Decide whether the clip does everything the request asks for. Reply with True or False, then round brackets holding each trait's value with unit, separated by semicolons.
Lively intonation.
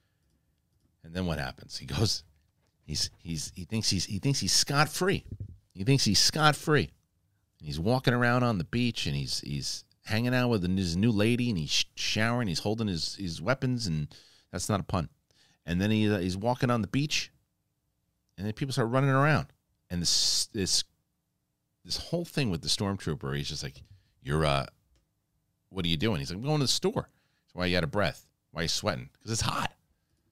True (6.4 semitones)